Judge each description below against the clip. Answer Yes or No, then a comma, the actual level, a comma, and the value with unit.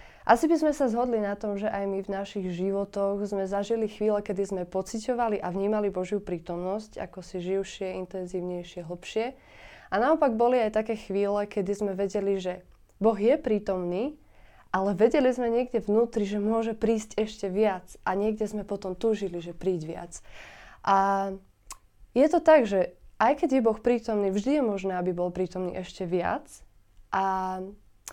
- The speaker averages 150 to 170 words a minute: Yes, fast, 165 wpm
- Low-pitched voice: No, high, 200 Hz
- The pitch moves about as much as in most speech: Yes, average, 3.0 semitones